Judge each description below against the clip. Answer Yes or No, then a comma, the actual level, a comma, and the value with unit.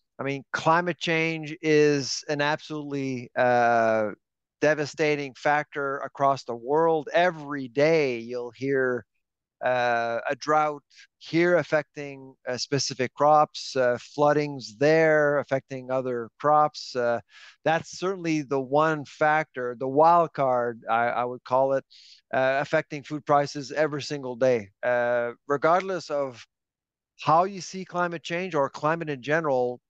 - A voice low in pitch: No, medium, 145 Hz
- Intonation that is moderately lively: Yes, average, 3.4 semitones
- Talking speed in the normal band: No, slow, 130 wpm